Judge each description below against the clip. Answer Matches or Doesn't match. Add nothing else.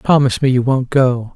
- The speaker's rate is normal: Doesn't match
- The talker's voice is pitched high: Doesn't match